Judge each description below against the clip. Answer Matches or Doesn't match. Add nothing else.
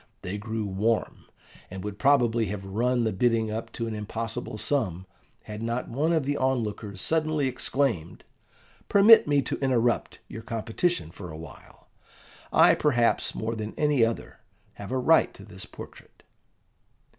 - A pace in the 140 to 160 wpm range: Matches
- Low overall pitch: Matches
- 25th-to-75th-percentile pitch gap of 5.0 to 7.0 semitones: Doesn't match